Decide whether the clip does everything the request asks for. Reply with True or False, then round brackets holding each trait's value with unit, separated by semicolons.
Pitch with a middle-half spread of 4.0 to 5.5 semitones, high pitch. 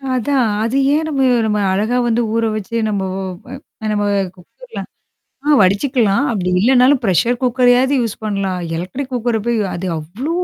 True (4.3 semitones; 230 Hz)